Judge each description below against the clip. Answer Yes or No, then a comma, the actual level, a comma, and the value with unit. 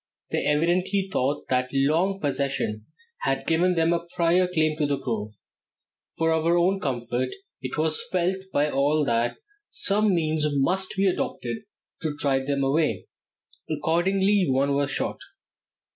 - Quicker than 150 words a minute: No, average, 145 wpm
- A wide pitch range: No, average, 4.6 semitones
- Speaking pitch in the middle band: Yes, medium, 155 Hz